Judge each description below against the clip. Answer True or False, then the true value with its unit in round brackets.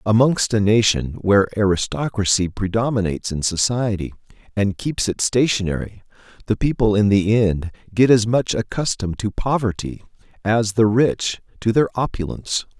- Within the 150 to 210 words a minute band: False (135 wpm)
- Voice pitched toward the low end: True (110 Hz)